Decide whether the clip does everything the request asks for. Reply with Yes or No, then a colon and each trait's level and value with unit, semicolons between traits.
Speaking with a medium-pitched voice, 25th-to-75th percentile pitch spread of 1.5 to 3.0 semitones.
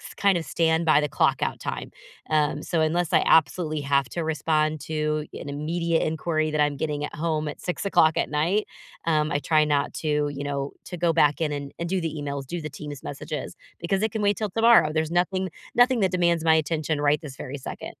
Yes: medium, 155 Hz; narrow, 2.5 semitones